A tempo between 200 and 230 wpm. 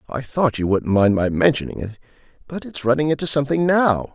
Yes: fast, 205 wpm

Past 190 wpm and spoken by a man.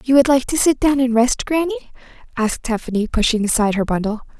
No: fast, 205 wpm; female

